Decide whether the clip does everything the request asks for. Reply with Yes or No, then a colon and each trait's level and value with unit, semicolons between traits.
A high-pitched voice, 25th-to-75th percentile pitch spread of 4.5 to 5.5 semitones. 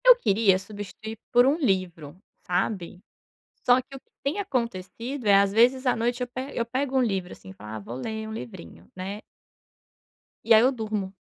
Yes: high, 220 Hz; average, 5.1 semitones